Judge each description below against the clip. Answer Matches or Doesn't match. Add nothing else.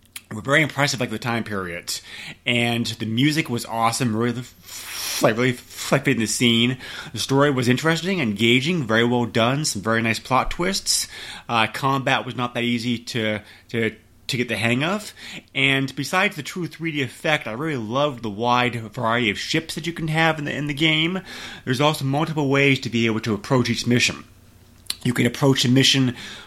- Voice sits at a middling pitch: Doesn't match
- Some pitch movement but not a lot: Matches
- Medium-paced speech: Matches